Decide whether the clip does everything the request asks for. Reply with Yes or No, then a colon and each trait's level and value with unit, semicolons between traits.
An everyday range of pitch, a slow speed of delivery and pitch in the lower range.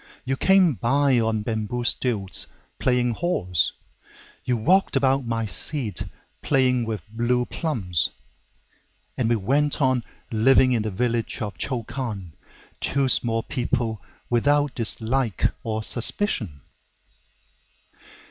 Yes: average, 3.6 semitones; slow, 100 wpm; low, 120 Hz